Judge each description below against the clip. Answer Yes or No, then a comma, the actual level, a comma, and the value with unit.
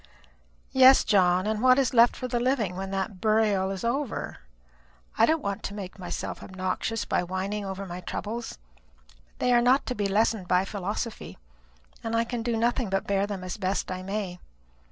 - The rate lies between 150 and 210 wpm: Yes, average, 190 wpm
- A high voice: Yes, high, 205 Hz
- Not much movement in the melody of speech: No, average, 3.8 semitones